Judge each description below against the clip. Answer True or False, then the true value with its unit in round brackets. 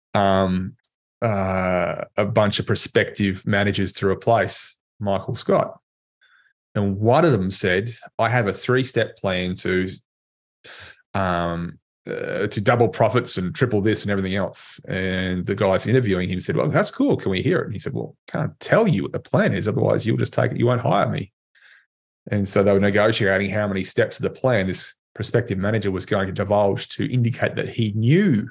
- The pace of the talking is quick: False (190 wpm)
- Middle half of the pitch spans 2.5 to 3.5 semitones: True (2.8 semitones)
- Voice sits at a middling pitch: False (100 Hz)